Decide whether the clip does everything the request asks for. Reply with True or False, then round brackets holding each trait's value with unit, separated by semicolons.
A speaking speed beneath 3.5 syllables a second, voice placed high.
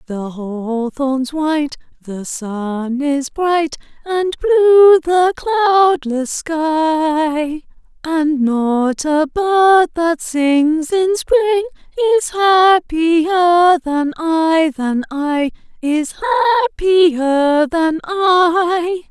True (2.7 syllables/s; 315 Hz)